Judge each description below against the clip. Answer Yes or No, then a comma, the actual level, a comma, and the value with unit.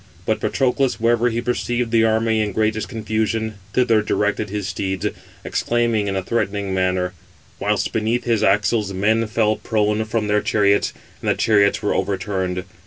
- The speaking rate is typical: Yes, average, 160 wpm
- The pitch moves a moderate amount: No, narrow, 2.1 semitones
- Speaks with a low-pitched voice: Yes, low, 110 Hz